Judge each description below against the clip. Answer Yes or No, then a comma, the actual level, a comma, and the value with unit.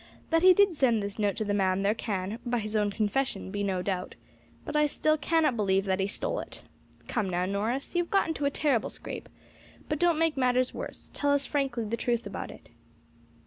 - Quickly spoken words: Yes, fast, 220 wpm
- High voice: Yes, high, 235 Hz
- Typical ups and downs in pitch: No, wide, 6.3 semitones